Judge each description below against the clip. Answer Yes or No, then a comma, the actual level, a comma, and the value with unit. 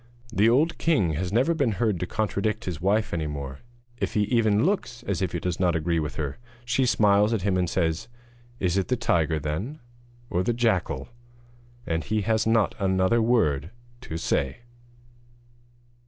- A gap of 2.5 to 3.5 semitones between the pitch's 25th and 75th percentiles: No, wide, 5.5 semitones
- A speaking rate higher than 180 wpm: No, average, 175 wpm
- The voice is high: No, low, 100 Hz